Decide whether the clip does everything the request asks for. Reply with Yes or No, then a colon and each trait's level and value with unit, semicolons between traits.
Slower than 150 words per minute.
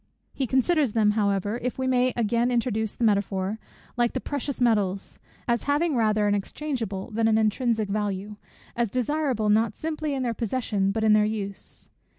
No: average, 170 wpm